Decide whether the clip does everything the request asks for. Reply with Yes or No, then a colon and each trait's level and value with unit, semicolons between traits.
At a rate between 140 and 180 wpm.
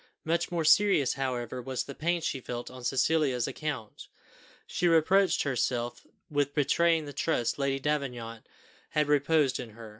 Yes: average, 150 wpm